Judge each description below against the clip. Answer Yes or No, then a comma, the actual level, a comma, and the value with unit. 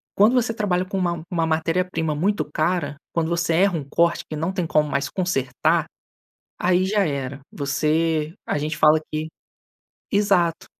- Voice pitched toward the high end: No, medium, 165 Hz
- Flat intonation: No, average, 3.2 semitones